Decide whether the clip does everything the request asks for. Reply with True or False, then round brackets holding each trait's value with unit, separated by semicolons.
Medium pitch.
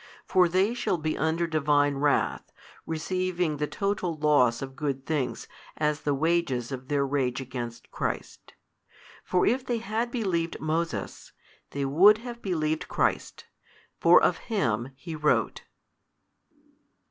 True (155 Hz)